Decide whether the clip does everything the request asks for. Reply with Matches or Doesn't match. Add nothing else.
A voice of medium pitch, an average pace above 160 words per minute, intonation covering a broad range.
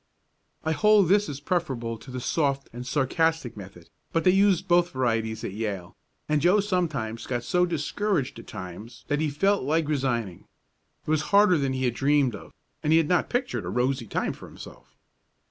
Matches